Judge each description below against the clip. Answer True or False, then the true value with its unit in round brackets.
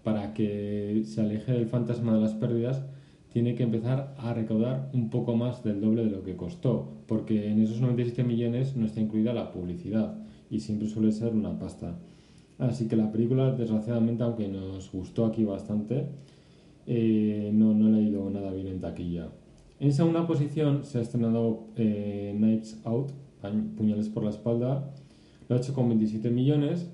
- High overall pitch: False (115 Hz)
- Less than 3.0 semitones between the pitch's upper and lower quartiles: True (2.5 semitones)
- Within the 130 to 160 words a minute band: False (175 wpm)